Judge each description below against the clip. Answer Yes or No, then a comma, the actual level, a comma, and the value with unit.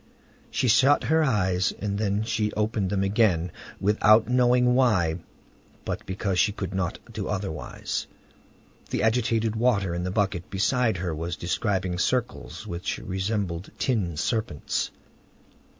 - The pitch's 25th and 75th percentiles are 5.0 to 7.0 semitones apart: No, average, 3.7 semitones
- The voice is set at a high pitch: No, low, 100 Hz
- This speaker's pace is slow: Yes, slow, 130 wpm